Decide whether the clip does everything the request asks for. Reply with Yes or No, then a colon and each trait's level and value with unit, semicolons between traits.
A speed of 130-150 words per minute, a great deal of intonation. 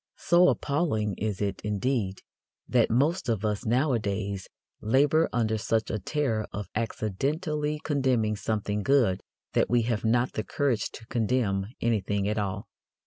No: average, 140 wpm; average, 4.3 semitones